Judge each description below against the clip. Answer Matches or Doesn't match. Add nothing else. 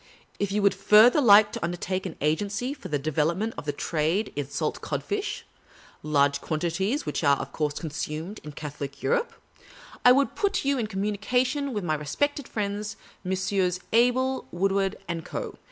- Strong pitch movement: Matches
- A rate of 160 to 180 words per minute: Matches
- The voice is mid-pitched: Doesn't match